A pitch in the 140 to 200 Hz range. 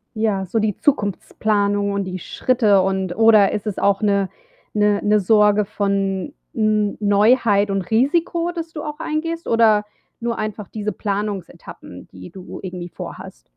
No: high, 210 Hz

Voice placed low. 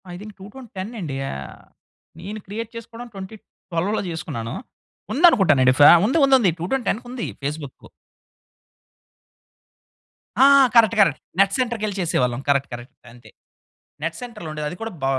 No: high, 195 Hz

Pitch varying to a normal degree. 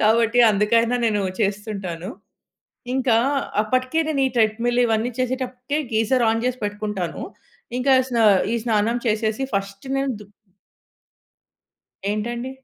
Yes: average, 3.0 semitones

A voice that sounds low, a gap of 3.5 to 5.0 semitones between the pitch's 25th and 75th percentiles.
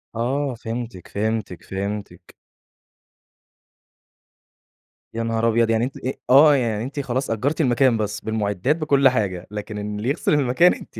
Yes: low, 115 Hz; average, 4.1 semitones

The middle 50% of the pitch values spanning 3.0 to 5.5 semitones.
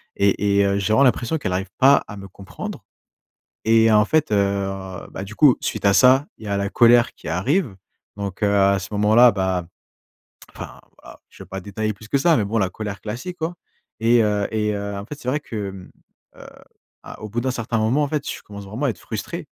Yes: average, 3.4 semitones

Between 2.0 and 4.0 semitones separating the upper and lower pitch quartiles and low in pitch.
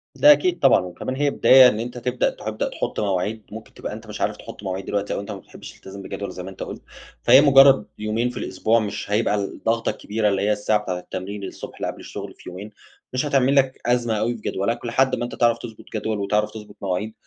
Yes: average, 3.4 semitones; low, 110 Hz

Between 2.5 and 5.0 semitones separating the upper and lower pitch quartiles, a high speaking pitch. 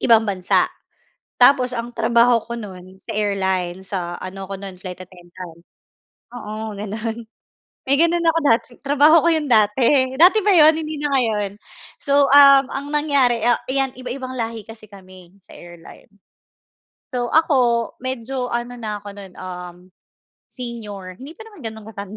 No: wide, 5.4 semitones; high, 230 Hz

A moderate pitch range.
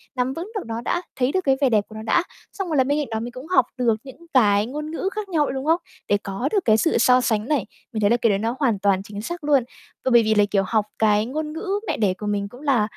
No: wide, 5.8 semitones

